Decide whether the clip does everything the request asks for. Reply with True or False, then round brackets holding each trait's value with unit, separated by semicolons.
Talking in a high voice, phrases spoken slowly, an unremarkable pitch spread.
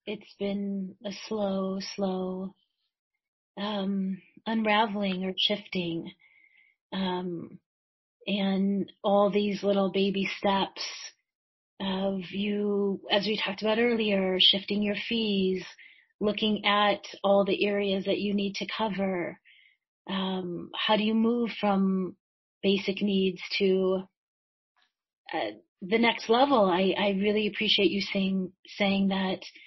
False (200 Hz; 115 wpm; 1.5 semitones)